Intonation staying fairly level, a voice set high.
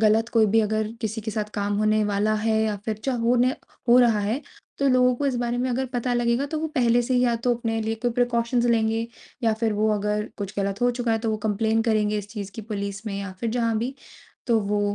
Yes: narrow, 2.3 semitones; high, 225 Hz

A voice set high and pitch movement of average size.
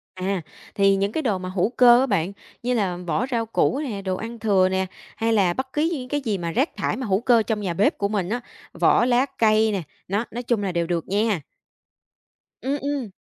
Yes: high, 215 Hz; average, 4.3 semitones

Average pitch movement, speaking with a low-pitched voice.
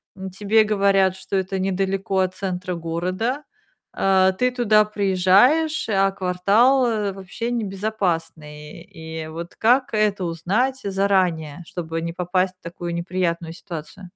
No: average, 3.1 semitones; high, 190 Hz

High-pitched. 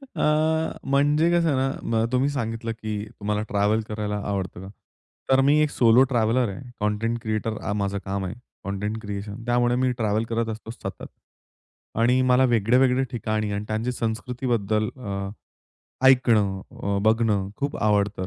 No: low, 110 Hz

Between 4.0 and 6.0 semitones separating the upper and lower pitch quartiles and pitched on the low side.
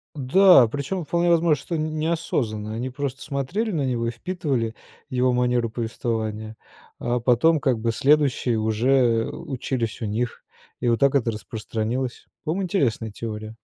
Yes: average, 4.8 semitones; low, 125 Hz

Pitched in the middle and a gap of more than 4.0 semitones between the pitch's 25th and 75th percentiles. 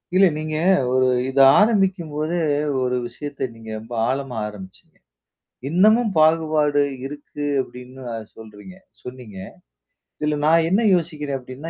Yes: medium, 145 Hz; average, 4.5 semitones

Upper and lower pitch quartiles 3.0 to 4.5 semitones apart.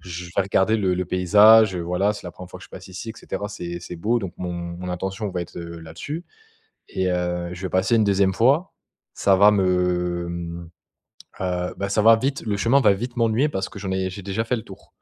Yes: average, 3.3 semitones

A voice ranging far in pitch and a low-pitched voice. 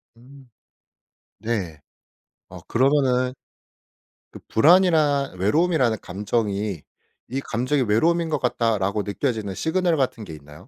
Yes: wide, 5.8 semitones; low, 125 Hz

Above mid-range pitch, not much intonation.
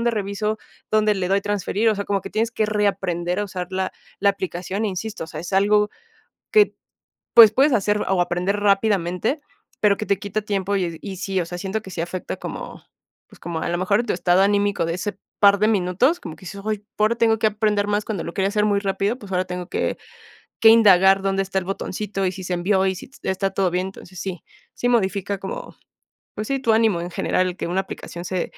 Yes: high, 195 Hz; narrow, 2.3 semitones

